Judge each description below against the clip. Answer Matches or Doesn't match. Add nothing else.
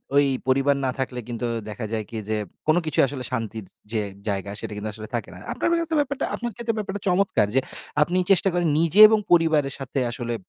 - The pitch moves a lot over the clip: Matches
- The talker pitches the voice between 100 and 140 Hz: Matches